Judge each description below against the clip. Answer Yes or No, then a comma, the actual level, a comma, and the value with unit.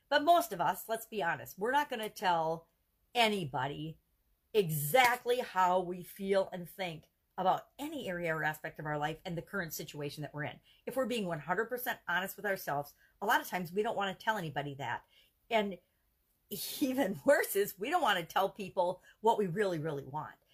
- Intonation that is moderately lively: No, wide, 5.9 semitones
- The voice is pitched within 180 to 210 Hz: Yes, medium, 185 Hz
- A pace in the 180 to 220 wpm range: Yes, average, 195 wpm